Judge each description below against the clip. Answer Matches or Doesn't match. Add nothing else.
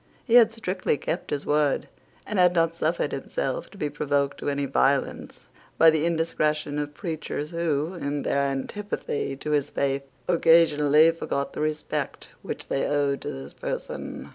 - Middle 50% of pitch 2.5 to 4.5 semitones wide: Matches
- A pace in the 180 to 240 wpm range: Doesn't match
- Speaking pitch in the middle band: Matches